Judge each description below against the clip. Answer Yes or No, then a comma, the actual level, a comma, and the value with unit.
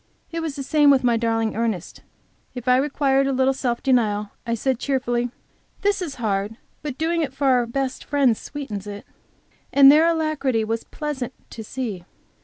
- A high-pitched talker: Yes, very high, 260 Hz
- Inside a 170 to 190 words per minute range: Yes, average, 180 wpm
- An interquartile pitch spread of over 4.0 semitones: No, average, 3.7 semitones